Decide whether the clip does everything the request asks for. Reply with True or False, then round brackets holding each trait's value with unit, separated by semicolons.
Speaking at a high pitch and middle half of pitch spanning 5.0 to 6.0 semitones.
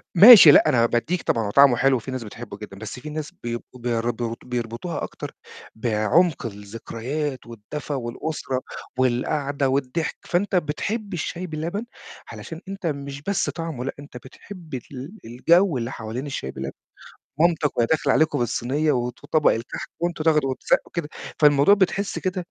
False (140 Hz; 5.4 semitones)